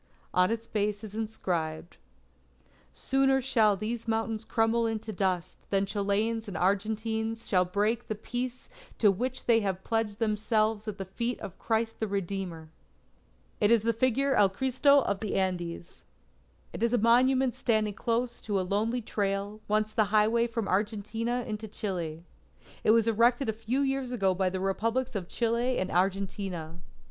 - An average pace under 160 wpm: No, average, 165 wpm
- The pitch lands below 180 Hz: No, high, 215 Hz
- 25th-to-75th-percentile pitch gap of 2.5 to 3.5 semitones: Yes, average, 2.9 semitones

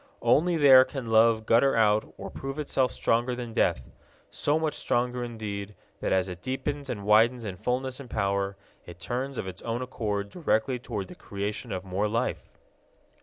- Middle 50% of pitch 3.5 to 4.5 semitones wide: Yes, average, 4.2 semitones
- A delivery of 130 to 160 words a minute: No, average, 175 wpm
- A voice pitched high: No, low, 115 Hz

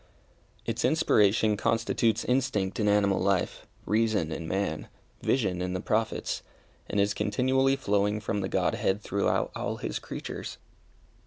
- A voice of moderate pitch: No, low, 105 Hz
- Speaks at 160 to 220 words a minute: No, slow, 135 wpm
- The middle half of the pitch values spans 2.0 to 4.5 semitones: Yes, average, 2.7 semitones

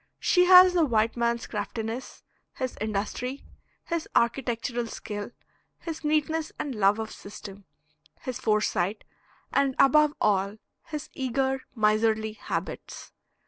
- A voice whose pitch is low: No, high, 235 Hz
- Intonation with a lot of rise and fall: No, average, 4.7 semitones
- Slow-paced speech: Yes, slow, 115 wpm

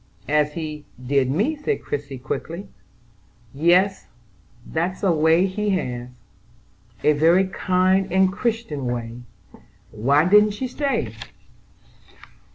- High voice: No, medium, 170 Hz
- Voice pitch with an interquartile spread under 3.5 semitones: No, average, 5.1 semitones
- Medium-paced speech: No, slow, 110 wpm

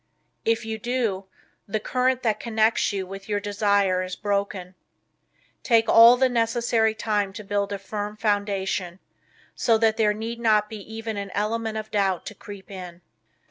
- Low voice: No, high, 210 Hz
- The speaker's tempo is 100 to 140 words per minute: No, average, 165 wpm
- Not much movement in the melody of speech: Yes, narrow, 2.1 semitones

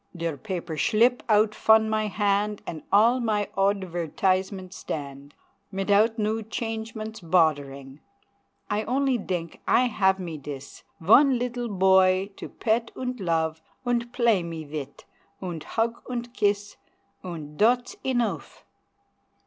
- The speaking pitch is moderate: No, high, 205 Hz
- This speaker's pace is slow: Yes, slow, 125 wpm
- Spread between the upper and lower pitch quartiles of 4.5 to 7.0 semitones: Yes, average, 5.0 semitones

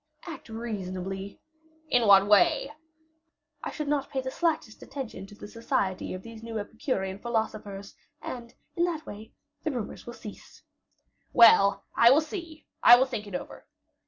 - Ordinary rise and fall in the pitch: Yes, average, 4.8 semitones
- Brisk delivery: No, average, 160 wpm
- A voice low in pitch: No, high, 225 Hz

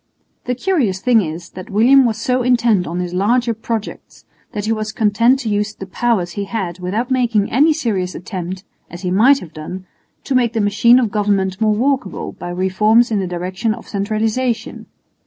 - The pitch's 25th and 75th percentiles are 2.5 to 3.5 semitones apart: No, average, 4.2 semitones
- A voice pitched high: Yes, high, 215 Hz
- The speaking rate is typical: Yes, average, 190 wpm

